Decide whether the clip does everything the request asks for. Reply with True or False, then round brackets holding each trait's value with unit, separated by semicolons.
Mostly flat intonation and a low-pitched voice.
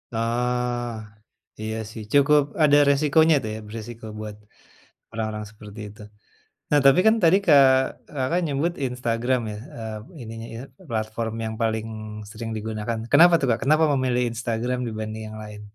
False (3.7 semitones; 115 Hz)